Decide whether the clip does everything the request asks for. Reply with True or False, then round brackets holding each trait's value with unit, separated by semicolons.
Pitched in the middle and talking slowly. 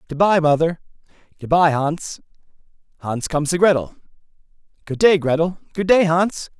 True (165 Hz; 125 wpm)